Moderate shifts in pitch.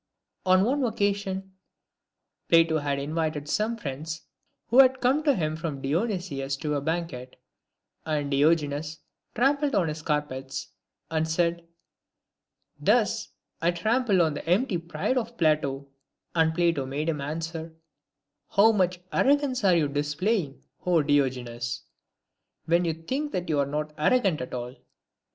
Yes: average, 4.8 semitones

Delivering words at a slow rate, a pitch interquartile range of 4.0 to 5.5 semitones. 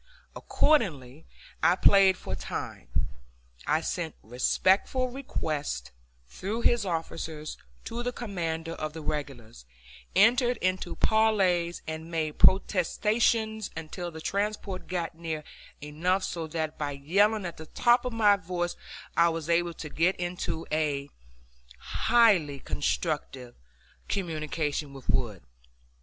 Yes: slow, 120 wpm; average, 4.6 semitones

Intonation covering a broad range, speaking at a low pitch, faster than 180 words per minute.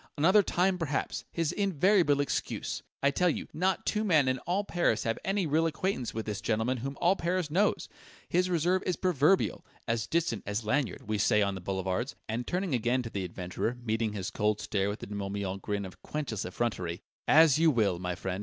Yes: wide, 8.7 semitones; low, 130 Hz; average, 200 wpm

